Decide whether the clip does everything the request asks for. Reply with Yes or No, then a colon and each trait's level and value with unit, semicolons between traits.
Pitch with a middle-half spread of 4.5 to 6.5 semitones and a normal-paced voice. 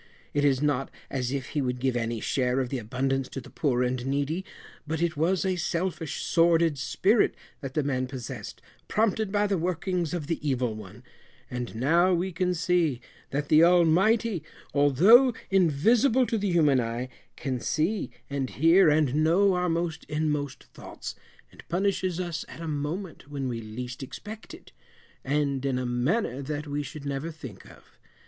Yes: average, 5.2 semitones; average, 175 wpm